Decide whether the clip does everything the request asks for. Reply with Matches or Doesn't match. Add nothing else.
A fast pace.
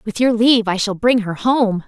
Matches